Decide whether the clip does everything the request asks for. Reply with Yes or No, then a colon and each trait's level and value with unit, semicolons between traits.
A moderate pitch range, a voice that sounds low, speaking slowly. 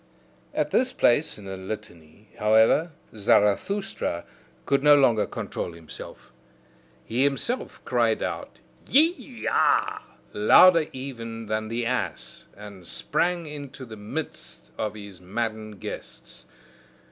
No: wide, 6.2 semitones; low, 115 Hz; slow, 115 wpm